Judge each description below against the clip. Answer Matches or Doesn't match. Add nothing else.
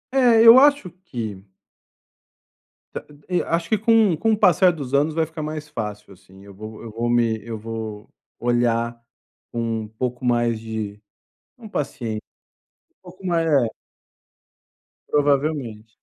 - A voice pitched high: Doesn't match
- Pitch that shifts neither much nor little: Doesn't match